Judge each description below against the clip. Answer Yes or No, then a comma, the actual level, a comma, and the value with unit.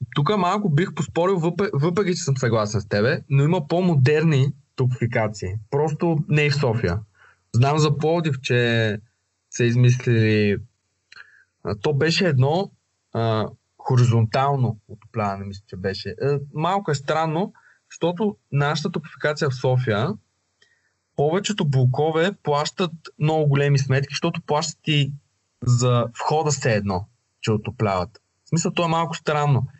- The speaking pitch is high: No, medium, 140 Hz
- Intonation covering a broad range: Yes, wide, 6.0 semitones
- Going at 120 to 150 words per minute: Yes, average, 130 wpm